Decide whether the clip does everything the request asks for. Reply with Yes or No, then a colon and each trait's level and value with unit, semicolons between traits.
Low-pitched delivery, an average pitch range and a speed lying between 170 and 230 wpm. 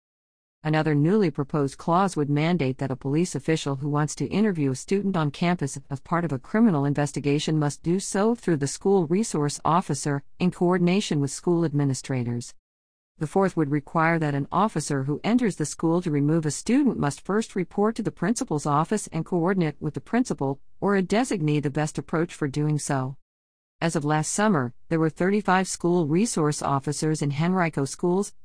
No: medium, 155 Hz; average, 4.2 semitones; average, 180 wpm